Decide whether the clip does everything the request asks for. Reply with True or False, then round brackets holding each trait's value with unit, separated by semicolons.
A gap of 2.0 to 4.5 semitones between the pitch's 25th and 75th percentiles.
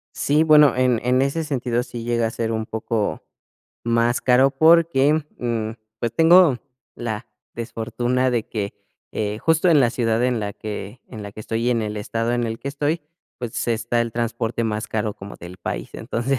True (2.8 semitones)